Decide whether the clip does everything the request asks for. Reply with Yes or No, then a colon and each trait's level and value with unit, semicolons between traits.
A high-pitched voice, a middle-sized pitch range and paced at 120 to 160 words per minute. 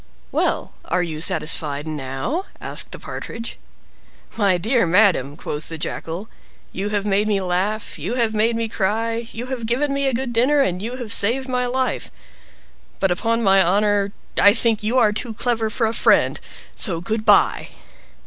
No: high, 215 Hz; average, 3.9 semitones; average, 175 wpm